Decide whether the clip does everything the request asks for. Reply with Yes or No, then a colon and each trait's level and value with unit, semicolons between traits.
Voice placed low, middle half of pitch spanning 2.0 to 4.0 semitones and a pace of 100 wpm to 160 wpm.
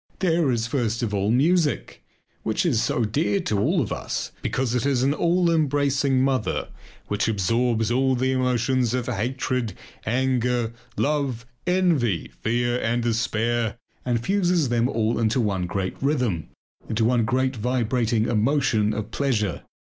Yes: low, 120 Hz; average, 3.2 semitones; average, 150 wpm